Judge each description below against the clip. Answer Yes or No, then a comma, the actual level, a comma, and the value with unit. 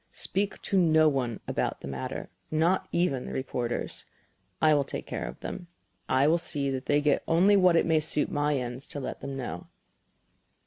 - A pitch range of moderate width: Yes, average, 4.2 semitones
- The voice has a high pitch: No, medium, 145 Hz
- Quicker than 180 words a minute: Yes, average, 190 wpm